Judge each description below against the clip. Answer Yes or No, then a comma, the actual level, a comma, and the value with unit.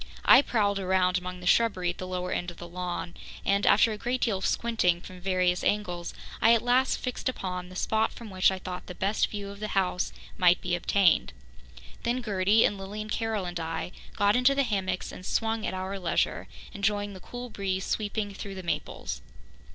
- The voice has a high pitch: Yes, high, 195 Hz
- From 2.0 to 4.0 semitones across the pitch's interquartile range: Yes, average, 2.9 semitones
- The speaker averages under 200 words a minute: No, fast, 205 wpm